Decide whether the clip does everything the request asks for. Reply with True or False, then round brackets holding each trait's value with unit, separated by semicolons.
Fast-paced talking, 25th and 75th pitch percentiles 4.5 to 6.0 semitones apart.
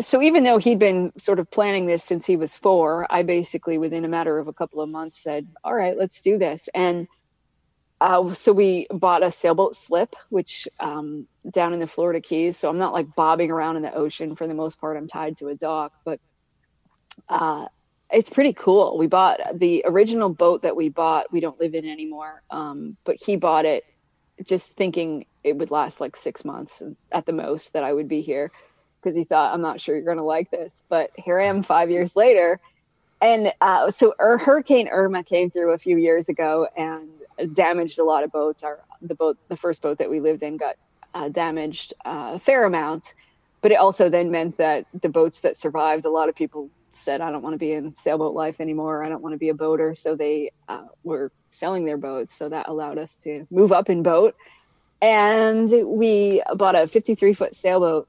False (215 wpm; 3.2 semitones)